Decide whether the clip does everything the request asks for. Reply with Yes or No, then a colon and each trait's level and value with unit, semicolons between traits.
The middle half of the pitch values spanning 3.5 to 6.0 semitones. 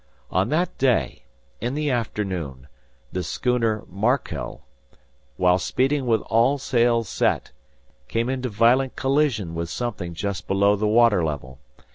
Yes: wide, 5.4 semitones